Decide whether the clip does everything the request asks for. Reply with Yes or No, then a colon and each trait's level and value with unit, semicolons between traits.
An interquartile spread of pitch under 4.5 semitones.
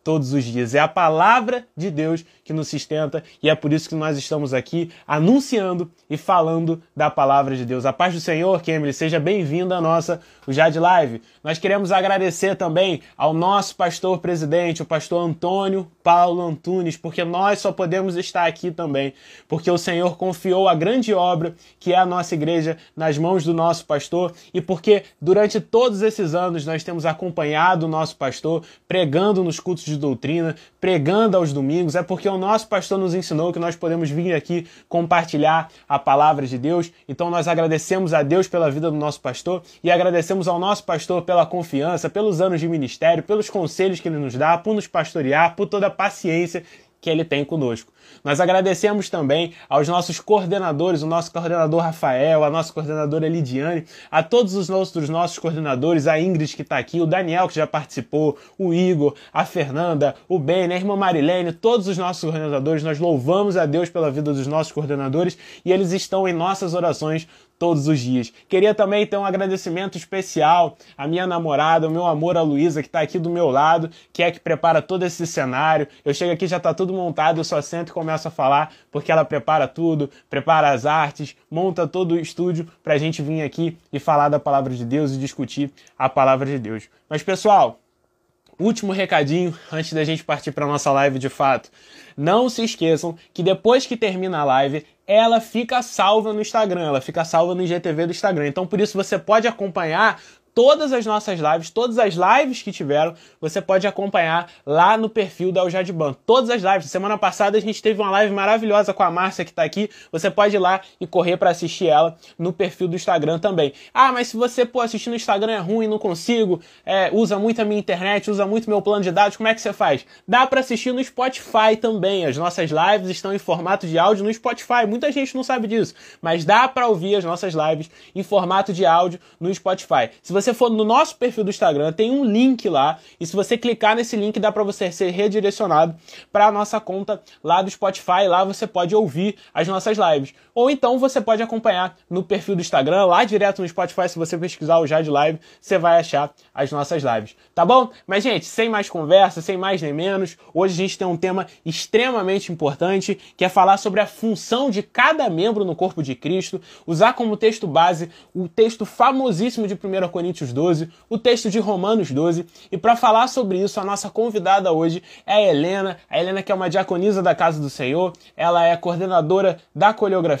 Yes: average, 3.9 semitones